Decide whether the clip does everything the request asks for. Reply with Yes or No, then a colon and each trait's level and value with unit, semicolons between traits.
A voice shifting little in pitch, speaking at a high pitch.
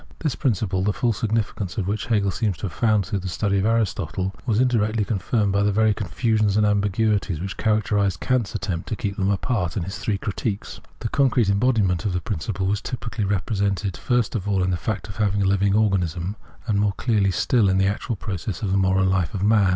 No: narrow, 2.3 semitones; low, 100 Hz